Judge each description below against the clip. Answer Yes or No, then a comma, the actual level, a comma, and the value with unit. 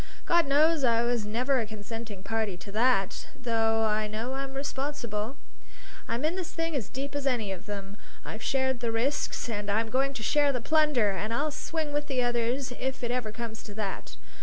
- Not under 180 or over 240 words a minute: Yes, average, 200 wpm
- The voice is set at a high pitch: Yes, high, 240 Hz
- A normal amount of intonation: Yes, average, 4.1 semitones